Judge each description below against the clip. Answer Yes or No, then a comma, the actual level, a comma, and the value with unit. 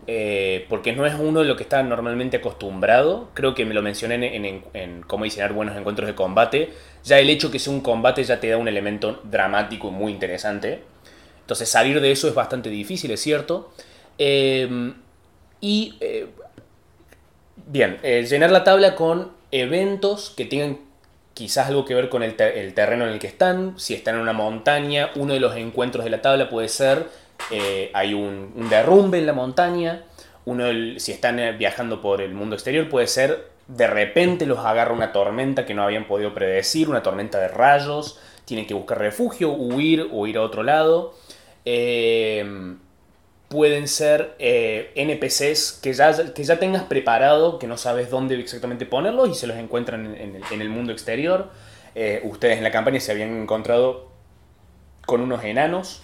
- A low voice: Yes, low, 125 Hz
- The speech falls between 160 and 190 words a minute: Yes, average, 185 wpm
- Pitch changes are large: Yes, wide, 6.1 semitones